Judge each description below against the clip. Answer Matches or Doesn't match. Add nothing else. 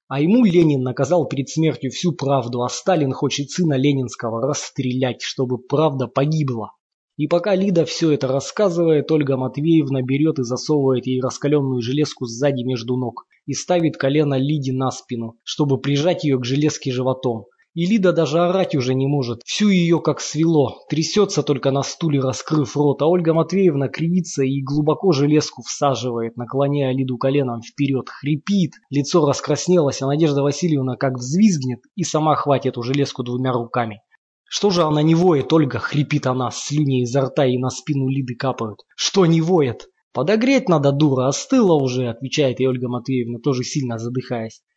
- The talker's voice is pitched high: Doesn't match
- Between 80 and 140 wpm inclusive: Doesn't match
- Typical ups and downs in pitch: Matches